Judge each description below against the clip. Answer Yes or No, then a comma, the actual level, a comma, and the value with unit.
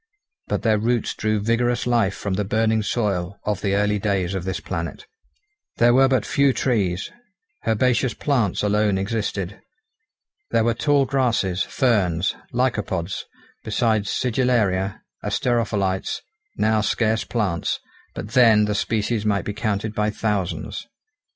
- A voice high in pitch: No, low, 105 Hz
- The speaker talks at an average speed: No, slow, 130 wpm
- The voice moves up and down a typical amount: Yes, average, 3.1 semitones